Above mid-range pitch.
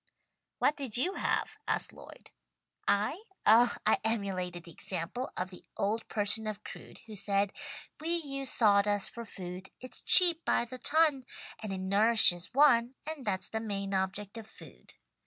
Yes: high, 215 Hz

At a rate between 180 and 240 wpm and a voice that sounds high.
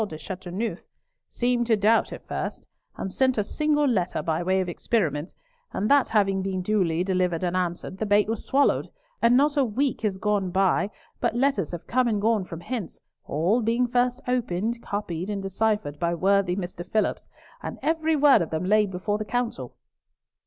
Yes: average, 185 wpm; high, 205 Hz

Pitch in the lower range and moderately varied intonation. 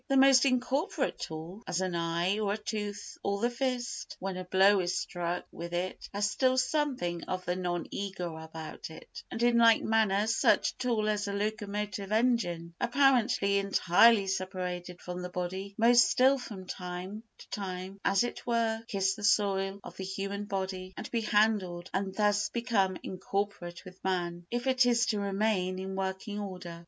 No: high, 200 Hz; average, 3.4 semitones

